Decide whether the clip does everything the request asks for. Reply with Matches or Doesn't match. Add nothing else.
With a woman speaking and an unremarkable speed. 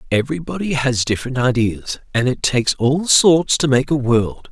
Doesn't match